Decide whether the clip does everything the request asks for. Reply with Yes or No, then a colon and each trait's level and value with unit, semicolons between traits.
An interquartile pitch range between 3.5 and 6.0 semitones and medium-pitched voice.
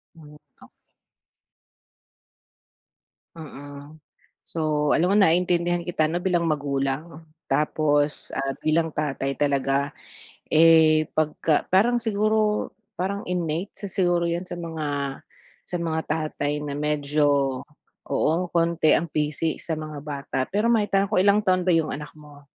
No: average, 3.1 semitones; medium, 155 Hz